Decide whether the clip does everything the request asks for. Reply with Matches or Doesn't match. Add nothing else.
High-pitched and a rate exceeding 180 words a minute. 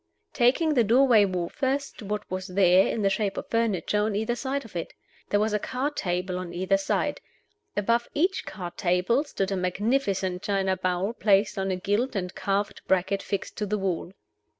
Matches